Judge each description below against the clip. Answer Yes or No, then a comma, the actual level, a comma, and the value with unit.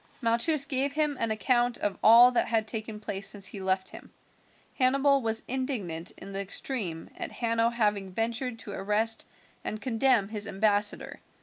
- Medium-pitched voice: No, high, 225 Hz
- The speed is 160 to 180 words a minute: Yes, average, 165 wpm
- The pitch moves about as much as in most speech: Yes, average, 3.6 semitones